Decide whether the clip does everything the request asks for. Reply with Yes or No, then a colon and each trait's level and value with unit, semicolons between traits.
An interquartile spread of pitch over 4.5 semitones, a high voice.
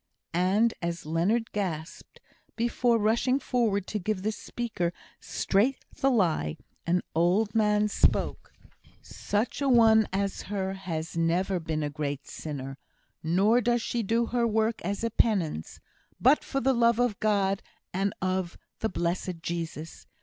Yes: average, 5.0 semitones; high, 200 Hz